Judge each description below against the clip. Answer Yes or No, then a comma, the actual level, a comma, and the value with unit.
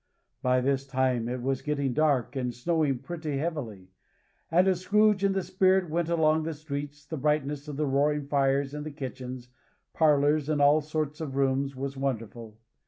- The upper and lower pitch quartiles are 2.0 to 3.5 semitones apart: Yes, average, 2.8 semitones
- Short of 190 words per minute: Yes, average, 170 wpm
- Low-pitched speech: No, medium, 145 Hz